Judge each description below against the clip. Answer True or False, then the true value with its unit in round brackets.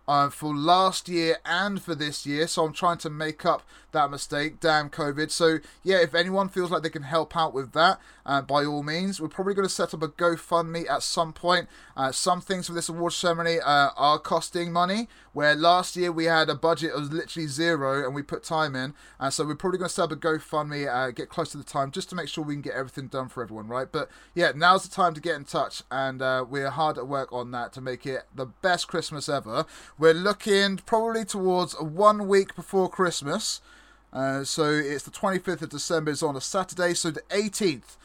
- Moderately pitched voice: True (160 Hz)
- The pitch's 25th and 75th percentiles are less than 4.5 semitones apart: True (3.5 semitones)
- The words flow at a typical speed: False (230 wpm)